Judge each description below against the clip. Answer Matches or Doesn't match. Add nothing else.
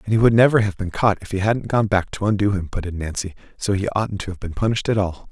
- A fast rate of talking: Matches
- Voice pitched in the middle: Doesn't match